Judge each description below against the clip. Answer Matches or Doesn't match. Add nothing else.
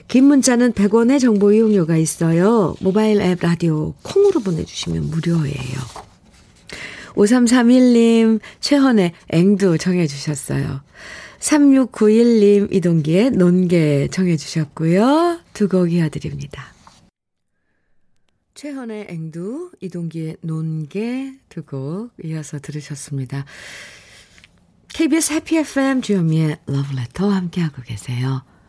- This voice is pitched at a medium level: Matches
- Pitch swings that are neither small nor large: Doesn't match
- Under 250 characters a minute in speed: Matches